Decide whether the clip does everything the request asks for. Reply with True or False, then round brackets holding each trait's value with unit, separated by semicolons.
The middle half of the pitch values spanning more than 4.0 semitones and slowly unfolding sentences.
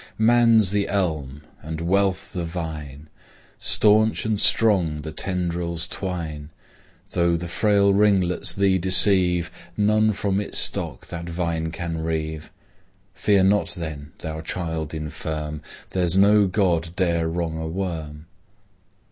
False (3.6 semitones; 125 wpm)